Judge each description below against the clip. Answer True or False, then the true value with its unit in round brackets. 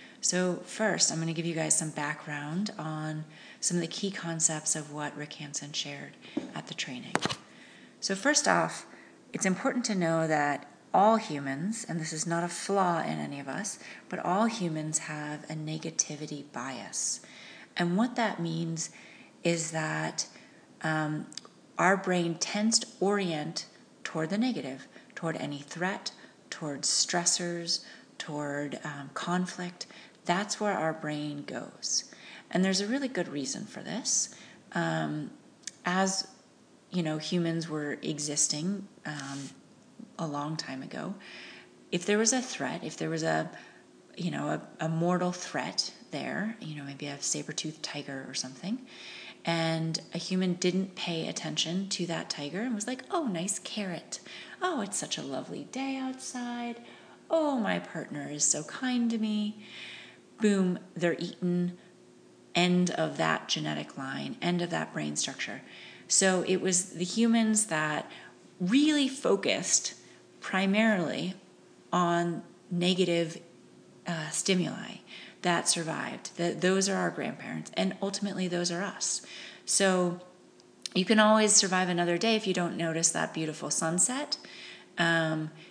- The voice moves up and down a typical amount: True (4.2 semitones)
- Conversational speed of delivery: True (145 wpm)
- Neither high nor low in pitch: True (175 Hz)